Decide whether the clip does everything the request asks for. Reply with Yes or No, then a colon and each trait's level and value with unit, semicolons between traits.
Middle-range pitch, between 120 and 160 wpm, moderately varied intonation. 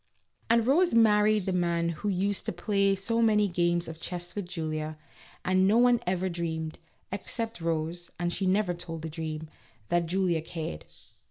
No: medium, 180 Hz; average, 170 wpm; average, 3.7 semitones